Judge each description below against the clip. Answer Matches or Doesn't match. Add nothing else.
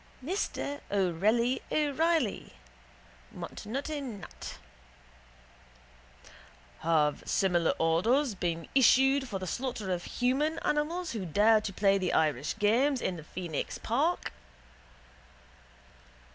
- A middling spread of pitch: Doesn't match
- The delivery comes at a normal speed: Doesn't match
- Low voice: Doesn't match